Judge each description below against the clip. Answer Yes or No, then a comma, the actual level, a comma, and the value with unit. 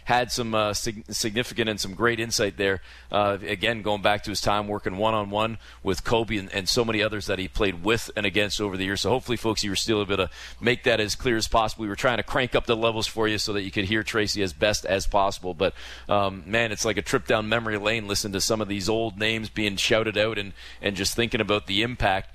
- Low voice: Yes, low, 105 Hz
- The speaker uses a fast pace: Yes, fast, 265 wpm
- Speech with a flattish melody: Yes, narrow, 2.0 semitones